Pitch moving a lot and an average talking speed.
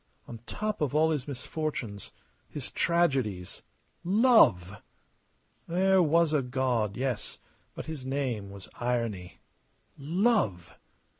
No: wide, 7.5 semitones; slow, 105 wpm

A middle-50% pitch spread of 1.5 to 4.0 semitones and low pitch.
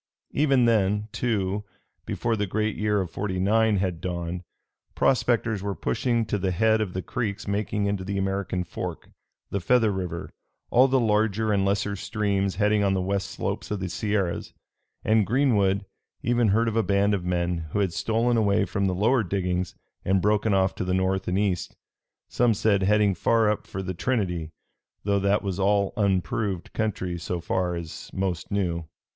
Yes: narrow, 2.5 semitones; low, 100 Hz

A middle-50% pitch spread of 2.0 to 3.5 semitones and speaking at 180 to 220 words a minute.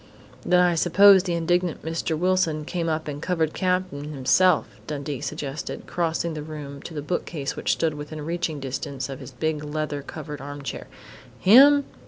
No: average, 3.2 semitones; average, 165 wpm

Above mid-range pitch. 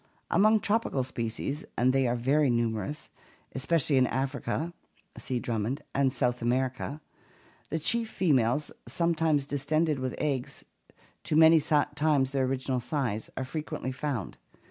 No: low, 135 Hz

